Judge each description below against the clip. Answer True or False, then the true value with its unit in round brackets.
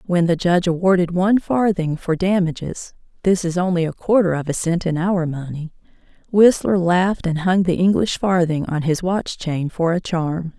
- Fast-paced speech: False (185 wpm)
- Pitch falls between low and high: True (175 Hz)